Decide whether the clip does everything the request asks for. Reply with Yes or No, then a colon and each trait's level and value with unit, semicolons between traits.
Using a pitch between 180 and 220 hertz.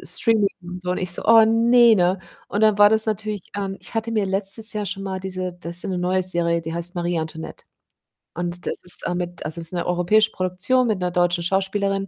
Yes: medium, 185 Hz